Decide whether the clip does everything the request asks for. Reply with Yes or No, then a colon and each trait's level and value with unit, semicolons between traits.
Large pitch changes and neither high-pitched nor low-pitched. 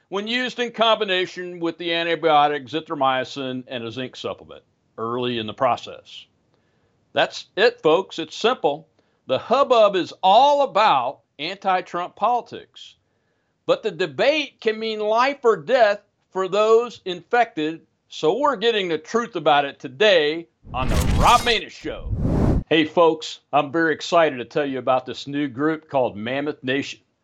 Yes: wide, 7.4 semitones; medium, 170 Hz